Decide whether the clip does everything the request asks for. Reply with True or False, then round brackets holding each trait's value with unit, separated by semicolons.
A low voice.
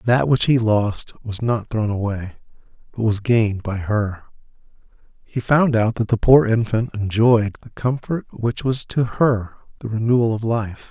True (110 Hz)